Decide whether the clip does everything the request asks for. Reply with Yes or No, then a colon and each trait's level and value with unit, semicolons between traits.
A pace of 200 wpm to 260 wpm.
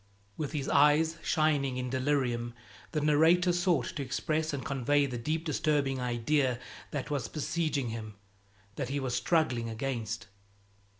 No: average, 140 wpm